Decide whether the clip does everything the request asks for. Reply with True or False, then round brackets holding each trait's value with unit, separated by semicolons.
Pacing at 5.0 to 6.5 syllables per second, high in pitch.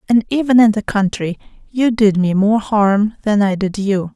False (4.5 syllables/s; 210 Hz)